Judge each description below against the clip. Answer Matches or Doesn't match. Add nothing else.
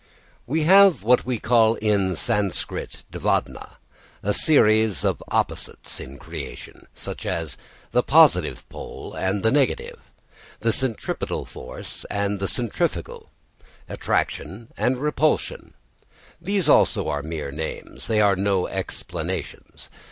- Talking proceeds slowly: Matches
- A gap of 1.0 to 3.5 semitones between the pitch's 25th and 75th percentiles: Doesn't match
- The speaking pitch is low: Matches